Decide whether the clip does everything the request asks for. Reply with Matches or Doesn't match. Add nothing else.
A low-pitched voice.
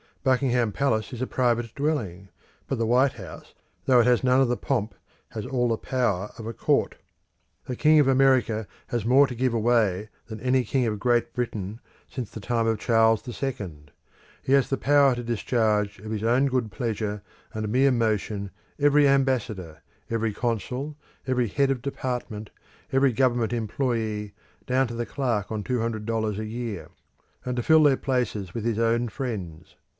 Matches